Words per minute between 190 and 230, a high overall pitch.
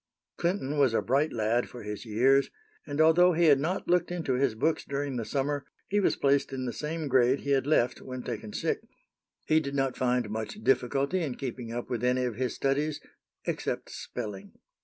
No: average, 200 wpm; low, 135 Hz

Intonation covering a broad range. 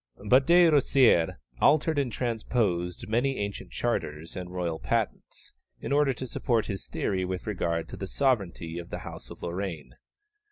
Yes: wide, 7.1 semitones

